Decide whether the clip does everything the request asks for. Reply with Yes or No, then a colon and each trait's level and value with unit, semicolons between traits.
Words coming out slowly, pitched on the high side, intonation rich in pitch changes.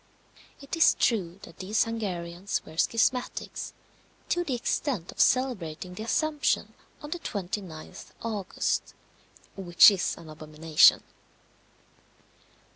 Yes: slow, 110 wpm; high, 200 Hz; wide, 6.5 semitones